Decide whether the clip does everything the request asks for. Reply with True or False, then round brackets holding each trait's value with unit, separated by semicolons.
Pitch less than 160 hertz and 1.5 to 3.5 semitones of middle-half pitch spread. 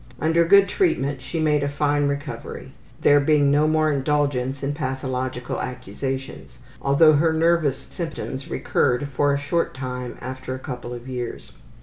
True (140 Hz; 2.9 semitones)